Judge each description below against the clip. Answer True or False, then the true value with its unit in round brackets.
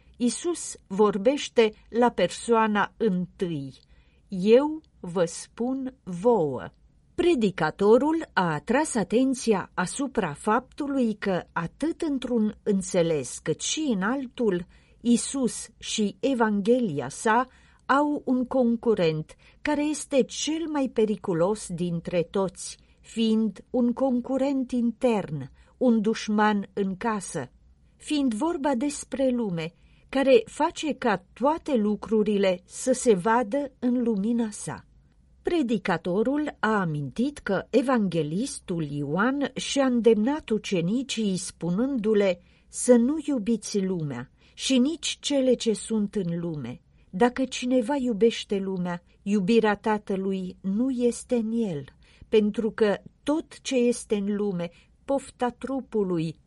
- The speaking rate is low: True (105 wpm)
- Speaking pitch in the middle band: False (225 Hz)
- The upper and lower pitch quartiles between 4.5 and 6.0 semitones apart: True (4.9 semitones)